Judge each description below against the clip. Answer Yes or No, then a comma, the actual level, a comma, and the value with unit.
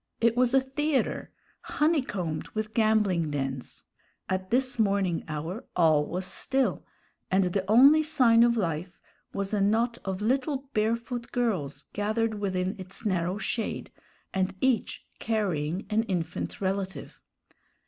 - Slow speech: Yes, slow, 130 wpm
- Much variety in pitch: No, average, 4.4 semitones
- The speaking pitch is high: Yes, high, 205 Hz